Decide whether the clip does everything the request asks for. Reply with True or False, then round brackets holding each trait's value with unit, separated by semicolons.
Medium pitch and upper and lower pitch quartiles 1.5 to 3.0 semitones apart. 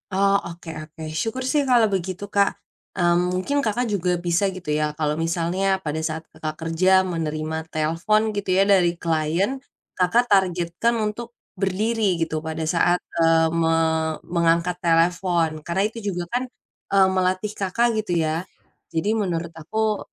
False (180 Hz; 3.5 semitones)